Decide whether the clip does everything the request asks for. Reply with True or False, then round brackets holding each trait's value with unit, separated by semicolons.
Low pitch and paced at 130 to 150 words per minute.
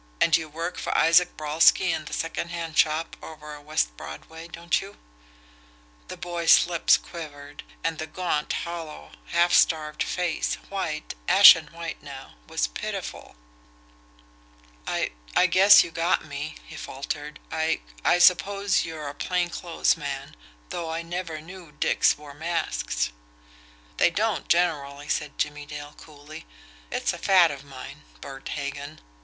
False (160 Hz; 145 wpm)